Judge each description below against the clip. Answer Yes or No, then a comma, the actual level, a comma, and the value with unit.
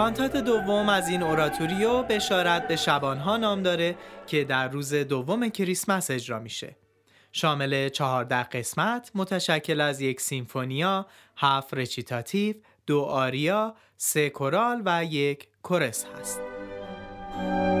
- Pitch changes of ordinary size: No, wide, 6.8 semitones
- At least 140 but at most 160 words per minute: No, average, 115 wpm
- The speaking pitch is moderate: Yes, medium, 150 Hz